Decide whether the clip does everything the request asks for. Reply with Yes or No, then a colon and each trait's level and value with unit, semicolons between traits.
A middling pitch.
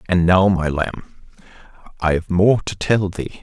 No: very low, 90 Hz